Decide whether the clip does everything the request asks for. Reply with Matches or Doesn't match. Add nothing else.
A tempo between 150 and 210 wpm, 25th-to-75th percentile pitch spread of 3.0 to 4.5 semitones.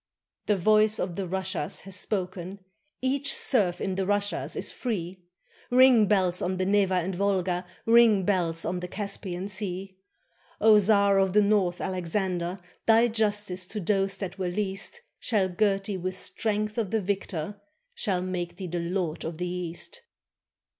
Doesn't match